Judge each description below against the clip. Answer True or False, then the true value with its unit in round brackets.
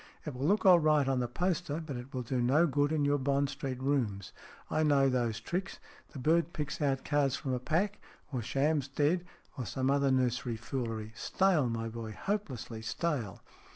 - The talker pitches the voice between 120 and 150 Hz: True (135 Hz)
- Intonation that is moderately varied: True (3.7 semitones)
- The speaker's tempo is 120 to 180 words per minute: False (190 wpm)